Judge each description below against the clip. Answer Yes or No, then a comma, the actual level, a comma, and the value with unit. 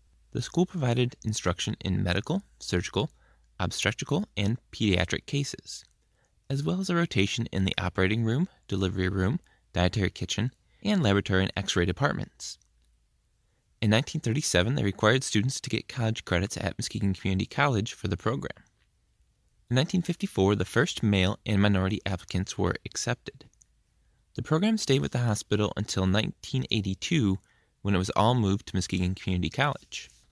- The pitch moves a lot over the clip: No, average, 4.6 semitones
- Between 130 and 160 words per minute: Yes, average, 145 wpm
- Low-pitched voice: Yes, low, 100 Hz